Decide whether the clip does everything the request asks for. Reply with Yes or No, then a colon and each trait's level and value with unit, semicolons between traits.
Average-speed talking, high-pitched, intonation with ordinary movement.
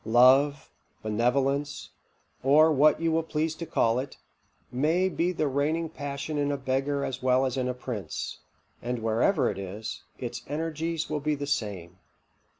No: average, 160 wpm; medium, 140 Hz; average, 3.5 semitones